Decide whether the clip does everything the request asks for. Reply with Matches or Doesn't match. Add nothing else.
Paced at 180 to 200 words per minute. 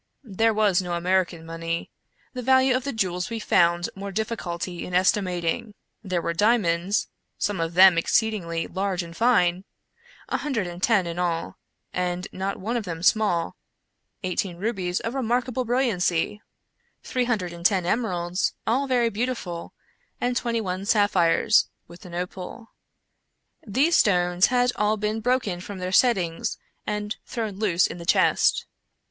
Doesn't match